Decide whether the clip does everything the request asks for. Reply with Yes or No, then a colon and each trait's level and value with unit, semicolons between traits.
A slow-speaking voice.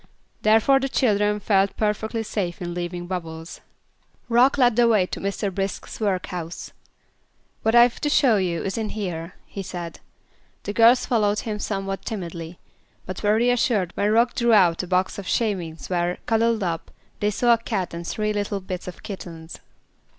No: average, 170 wpm